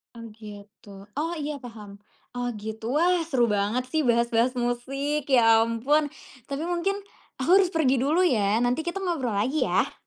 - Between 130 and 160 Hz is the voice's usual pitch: No, very high, 250 Hz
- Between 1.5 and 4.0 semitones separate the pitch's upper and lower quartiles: No, average, 5.2 semitones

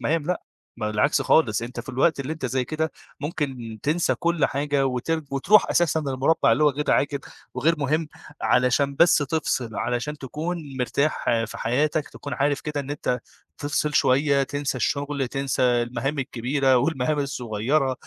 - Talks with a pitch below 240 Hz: Yes, medium, 140 Hz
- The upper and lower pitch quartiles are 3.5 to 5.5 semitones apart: No, average, 3.0 semitones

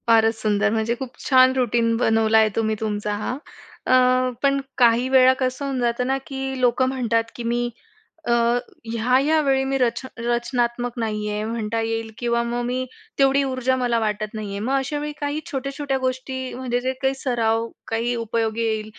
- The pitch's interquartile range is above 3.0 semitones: No, narrow, 2.5 semitones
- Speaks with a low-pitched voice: No, high, 240 Hz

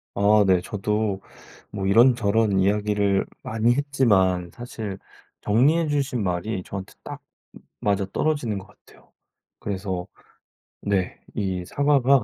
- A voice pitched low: Yes, low, 105 Hz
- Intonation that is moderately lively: Yes, average, 3.9 semitones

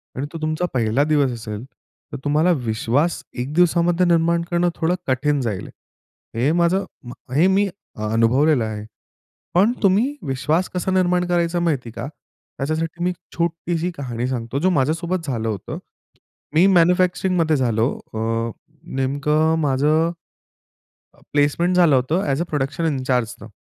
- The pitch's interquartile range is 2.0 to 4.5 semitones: No, average, 4.9 semitones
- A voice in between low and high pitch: Yes, medium, 155 Hz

